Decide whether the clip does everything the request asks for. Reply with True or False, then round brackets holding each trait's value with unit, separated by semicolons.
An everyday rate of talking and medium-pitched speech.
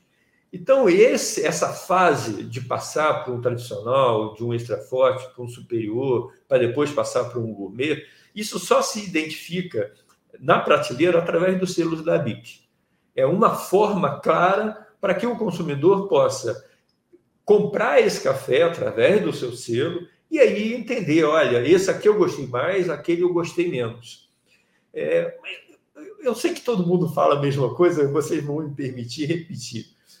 True (155 wpm; 175 Hz)